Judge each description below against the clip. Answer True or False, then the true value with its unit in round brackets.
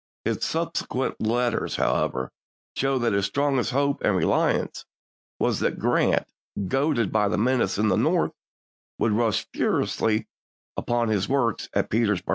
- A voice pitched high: False (115 Hz)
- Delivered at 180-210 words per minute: False (140 wpm)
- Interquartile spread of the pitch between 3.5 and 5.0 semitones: True (3.8 semitones)